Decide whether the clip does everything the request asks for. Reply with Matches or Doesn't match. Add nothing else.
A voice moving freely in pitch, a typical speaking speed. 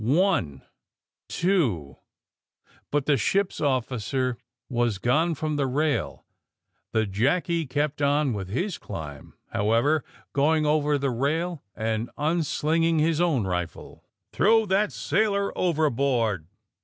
Doesn't match